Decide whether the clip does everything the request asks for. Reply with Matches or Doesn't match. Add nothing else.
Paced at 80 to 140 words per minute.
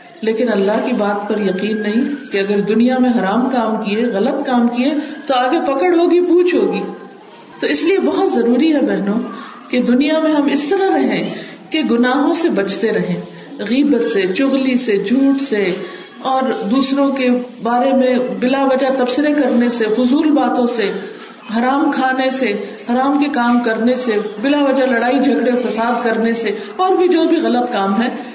Doesn't match